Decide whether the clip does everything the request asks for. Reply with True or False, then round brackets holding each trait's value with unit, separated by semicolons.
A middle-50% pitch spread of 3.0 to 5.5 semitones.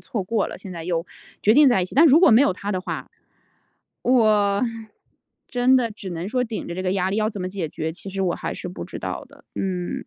True (4.0 semitones)